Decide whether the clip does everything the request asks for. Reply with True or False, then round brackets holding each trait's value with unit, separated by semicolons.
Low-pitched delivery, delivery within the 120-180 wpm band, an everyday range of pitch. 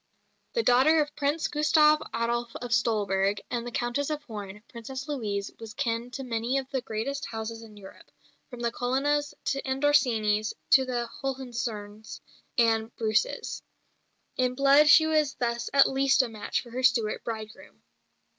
False (240 Hz; 155 wpm; 3.6 semitones)